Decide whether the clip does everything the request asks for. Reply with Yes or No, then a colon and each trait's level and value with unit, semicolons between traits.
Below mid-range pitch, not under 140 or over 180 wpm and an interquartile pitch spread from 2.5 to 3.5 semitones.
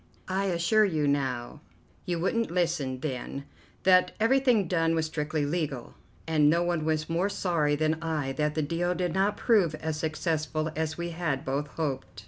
No: medium, 160 Hz; average, 170 wpm; average, 2.9 semitones